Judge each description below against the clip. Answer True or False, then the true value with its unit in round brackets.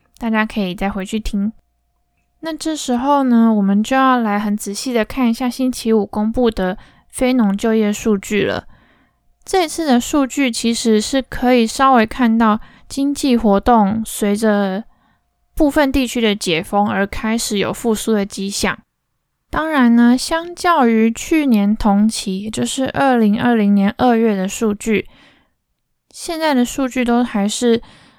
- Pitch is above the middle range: True (230 Hz)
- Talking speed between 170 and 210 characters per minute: False (225 characters per minute)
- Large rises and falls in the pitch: False (3.5 semitones)